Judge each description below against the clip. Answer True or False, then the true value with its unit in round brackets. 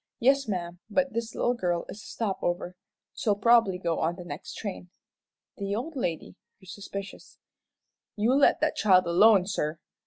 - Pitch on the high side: True (200 Hz)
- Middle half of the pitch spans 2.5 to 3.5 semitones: False (4.7 semitones)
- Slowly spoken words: False (165 wpm)